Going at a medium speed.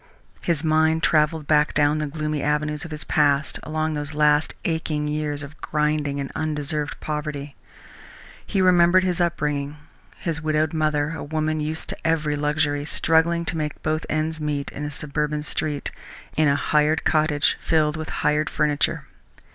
Yes: average, 160 wpm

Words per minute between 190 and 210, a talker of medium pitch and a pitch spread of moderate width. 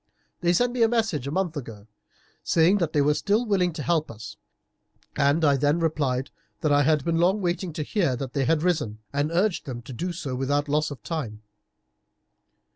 Yes: average, 200 wpm; medium, 155 Hz; average, 4.1 semitones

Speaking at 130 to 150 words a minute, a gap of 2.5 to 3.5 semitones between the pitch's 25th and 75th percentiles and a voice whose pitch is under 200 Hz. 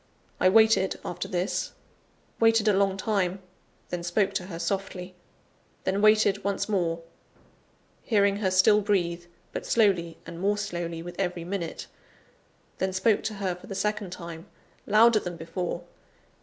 Yes: average, 145 wpm; average, 2.8 semitones; high, 190 Hz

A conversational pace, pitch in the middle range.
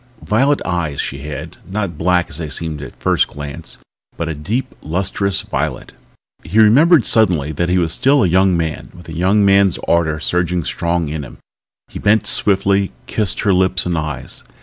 No: average, 180 wpm; very low, 90 Hz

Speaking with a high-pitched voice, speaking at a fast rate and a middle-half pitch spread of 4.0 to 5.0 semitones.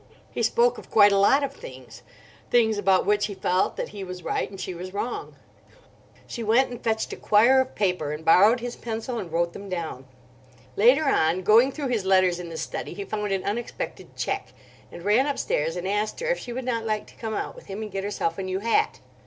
Yes: high, 205 Hz; fast, 225 wpm; average, 4.3 semitones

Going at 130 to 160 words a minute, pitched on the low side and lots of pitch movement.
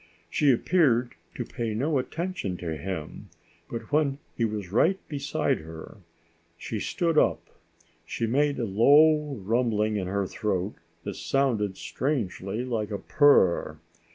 Yes: slow, 135 wpm; low, 115 Hz; wide, 6.2 semitones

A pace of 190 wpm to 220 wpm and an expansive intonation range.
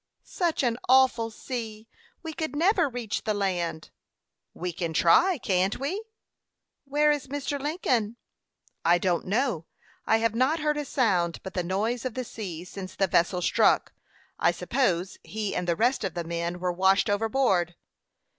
No: average, 165 wpm; wide, 6.8 semitones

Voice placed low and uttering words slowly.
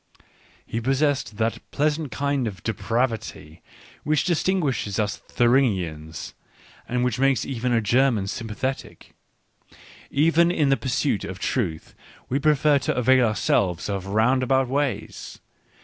Yes: low, 125 Hz; slow, 130 wpm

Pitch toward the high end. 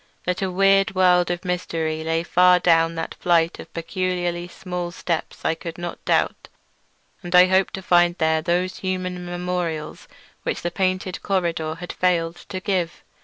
No: medium, 175 Hz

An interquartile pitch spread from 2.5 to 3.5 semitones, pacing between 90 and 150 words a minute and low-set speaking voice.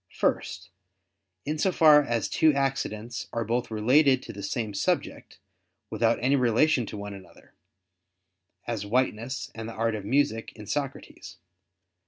No: average, 4.2 semitones; average, 145 wpm; low, 115 Hz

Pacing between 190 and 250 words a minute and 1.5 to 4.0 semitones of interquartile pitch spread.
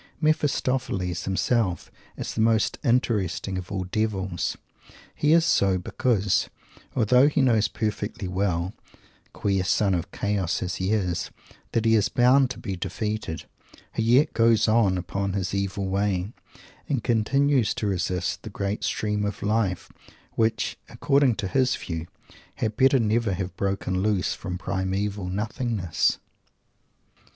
No: average, 140 wpm; average, 3.6 semitones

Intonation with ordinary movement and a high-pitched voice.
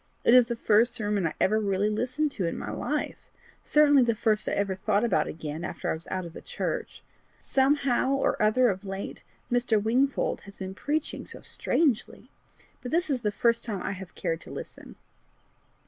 Yes: average, 4.8 semitones; high, 220 Hz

